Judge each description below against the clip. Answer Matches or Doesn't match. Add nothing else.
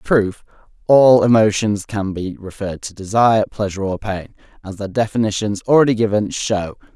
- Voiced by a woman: Doesn't match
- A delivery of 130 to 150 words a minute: Matches